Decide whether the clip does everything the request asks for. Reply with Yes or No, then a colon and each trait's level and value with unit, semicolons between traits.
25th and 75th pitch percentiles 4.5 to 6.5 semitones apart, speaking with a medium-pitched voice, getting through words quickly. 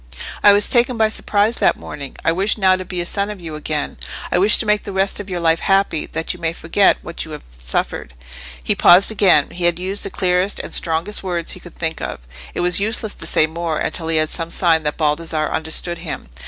No: average, 3.5 semitones; medium, 175 Hz; fast, 235 wpm